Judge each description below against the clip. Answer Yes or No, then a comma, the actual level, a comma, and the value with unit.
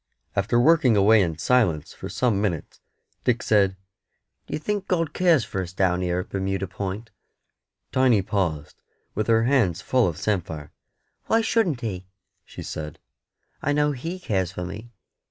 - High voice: No, low, 105 Hz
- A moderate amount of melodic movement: No, wide, 5.7 semitones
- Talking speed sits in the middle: Yes, average, 155 wpm